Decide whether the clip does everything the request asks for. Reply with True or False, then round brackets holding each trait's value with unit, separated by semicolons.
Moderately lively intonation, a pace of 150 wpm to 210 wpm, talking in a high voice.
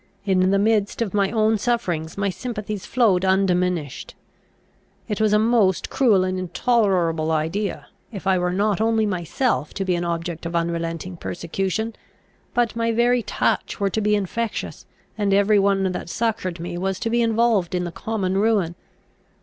True (3.7 semitones; 165 wpm; 195 Hz)